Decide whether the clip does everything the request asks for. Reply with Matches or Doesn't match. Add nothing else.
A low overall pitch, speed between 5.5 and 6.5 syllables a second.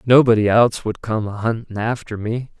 Doesn't match